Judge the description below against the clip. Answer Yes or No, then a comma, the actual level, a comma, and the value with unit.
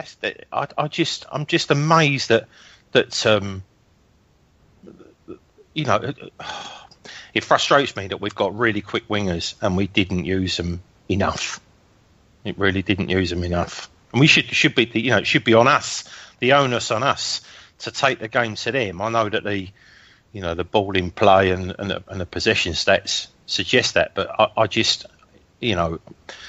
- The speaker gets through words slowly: No, average, 180 wpm